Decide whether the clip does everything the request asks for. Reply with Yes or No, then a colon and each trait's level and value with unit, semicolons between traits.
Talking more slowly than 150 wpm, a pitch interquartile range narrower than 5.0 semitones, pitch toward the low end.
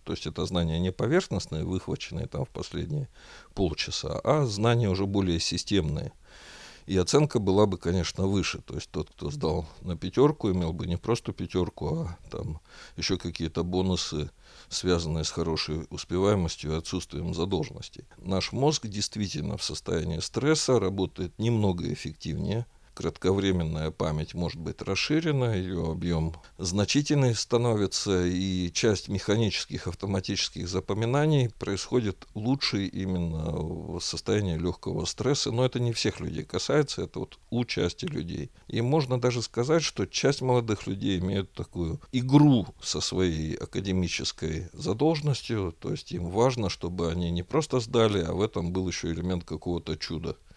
No: average, 140 wpm; average, 5.3 semitones; very low, 95 Hz